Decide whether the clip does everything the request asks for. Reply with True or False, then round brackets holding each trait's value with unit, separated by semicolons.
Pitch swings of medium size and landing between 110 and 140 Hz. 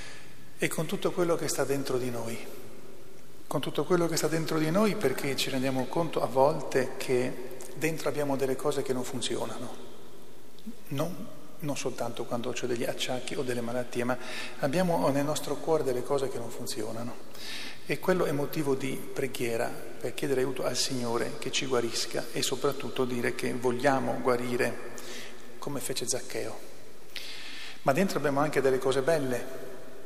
True (3.1 semitones; 135 Hz)